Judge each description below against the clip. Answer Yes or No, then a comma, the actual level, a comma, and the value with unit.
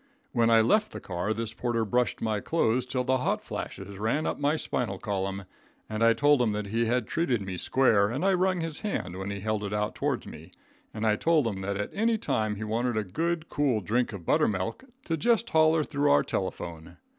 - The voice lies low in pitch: Yes, low, 115 Hz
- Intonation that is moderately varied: No, wide, 6.0 semitones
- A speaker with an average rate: No, fast, 220 wpm